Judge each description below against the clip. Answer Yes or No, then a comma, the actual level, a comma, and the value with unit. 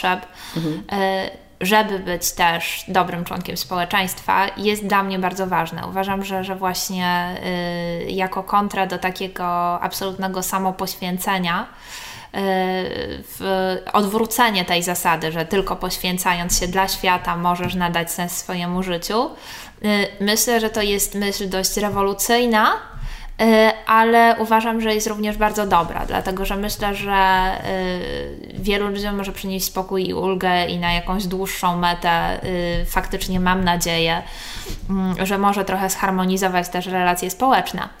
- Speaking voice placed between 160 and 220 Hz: Yes, high, 190 Hz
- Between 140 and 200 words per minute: No, average, 125 wpm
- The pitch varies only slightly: Yes, narrow, 2.1 semitones